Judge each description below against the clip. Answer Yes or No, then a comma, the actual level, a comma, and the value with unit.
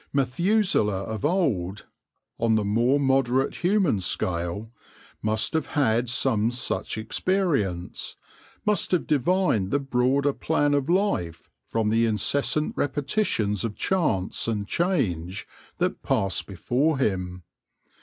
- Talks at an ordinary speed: No, slow, 120 wpm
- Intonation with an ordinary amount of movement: No, wide, 6.3 semitones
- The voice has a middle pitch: No, low, 125 Hz